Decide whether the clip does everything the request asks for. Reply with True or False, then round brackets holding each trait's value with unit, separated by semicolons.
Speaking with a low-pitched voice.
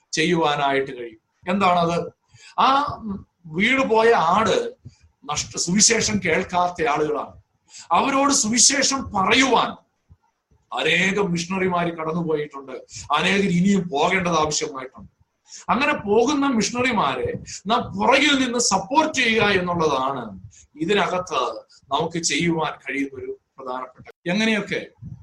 False (185 Hz)